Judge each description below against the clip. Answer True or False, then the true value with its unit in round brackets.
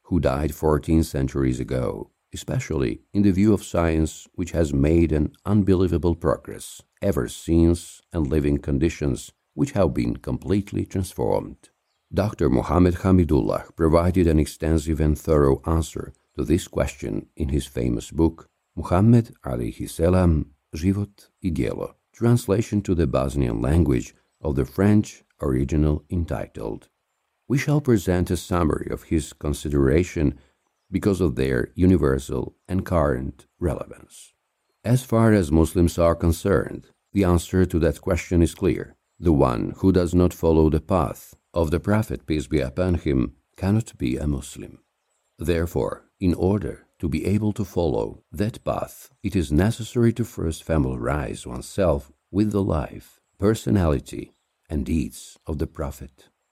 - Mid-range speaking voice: False (85 Hz)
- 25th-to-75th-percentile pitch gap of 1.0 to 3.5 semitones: False (4.3 semitones)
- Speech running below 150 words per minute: True (140 wpm)